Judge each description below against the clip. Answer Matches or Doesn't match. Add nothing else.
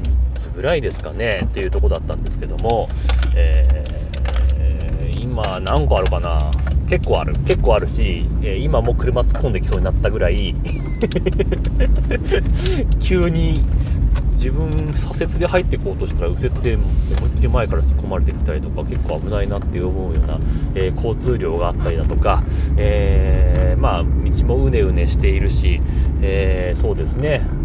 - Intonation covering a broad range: Doesn't match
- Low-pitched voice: Matches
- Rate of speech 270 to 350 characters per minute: Matches